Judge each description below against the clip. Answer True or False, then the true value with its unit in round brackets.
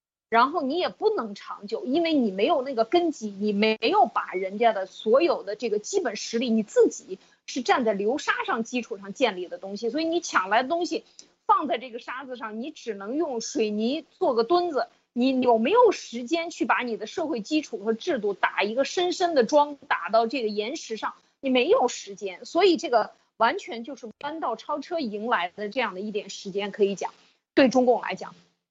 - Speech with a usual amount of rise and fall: False (6.6 semitones)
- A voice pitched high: True (245 Hz)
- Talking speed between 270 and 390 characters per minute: True (295 characters per minute)